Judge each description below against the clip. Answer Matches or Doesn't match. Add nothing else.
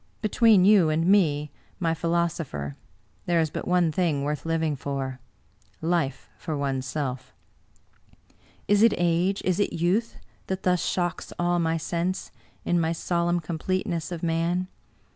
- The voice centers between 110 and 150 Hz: Doesn't match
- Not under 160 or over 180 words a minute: Doesn't match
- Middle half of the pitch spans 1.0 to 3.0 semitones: Matches